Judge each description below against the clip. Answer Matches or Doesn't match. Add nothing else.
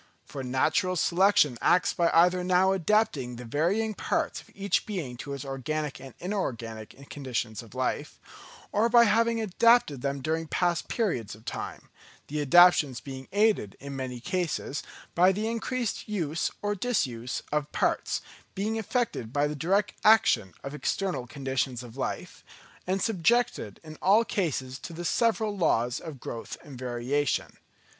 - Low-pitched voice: Doesn't match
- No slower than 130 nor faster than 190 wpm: Matches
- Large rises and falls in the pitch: Matches